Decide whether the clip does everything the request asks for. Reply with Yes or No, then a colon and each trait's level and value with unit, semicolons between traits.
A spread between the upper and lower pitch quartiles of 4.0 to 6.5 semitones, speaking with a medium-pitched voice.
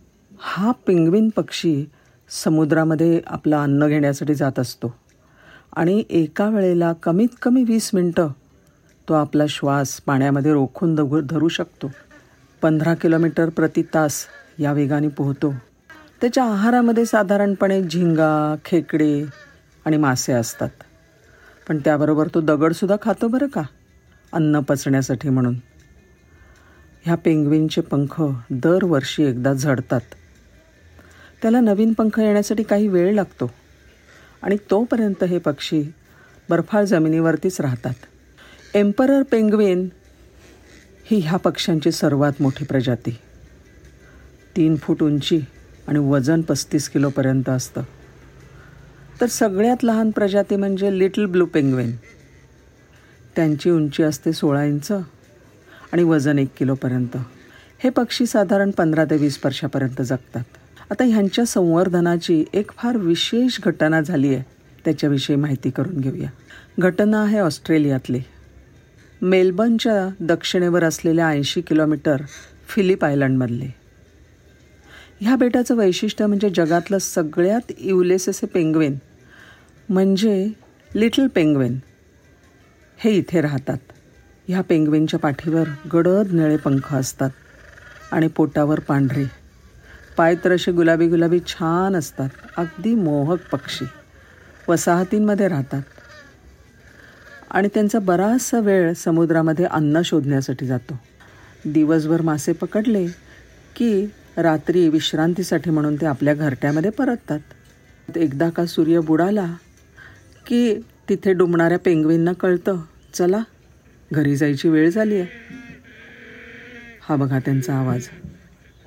Yes: average, 5.3 semitones; medium, 160 Hz